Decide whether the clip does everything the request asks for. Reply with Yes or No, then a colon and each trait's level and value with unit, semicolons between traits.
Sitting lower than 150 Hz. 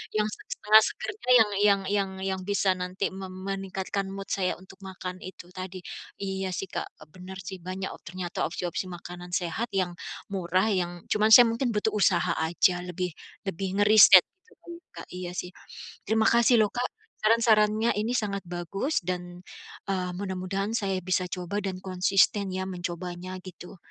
No: high, 190 Hz